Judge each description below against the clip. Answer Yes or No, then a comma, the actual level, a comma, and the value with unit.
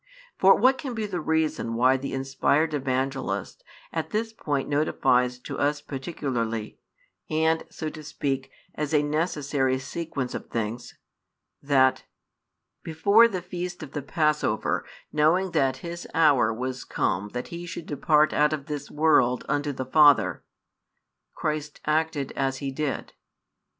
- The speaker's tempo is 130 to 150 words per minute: Yes, average, 140 wpm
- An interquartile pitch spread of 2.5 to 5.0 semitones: Yes, average, 3.3 semitones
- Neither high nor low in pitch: Yes, medium, 145 Hz